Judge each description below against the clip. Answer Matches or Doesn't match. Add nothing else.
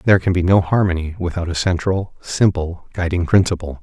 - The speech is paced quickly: Doesn't match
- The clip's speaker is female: Doesn't match